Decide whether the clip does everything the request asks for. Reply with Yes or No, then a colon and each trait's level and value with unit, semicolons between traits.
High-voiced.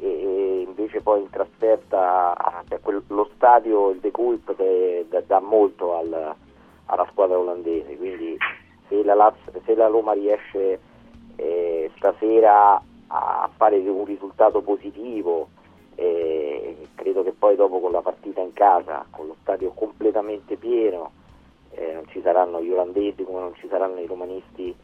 Yes: very high, 350 Hz